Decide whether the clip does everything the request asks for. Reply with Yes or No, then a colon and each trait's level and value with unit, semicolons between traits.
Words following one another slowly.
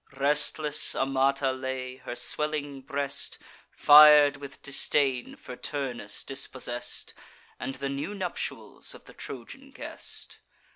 Yes: slow, 110 wpm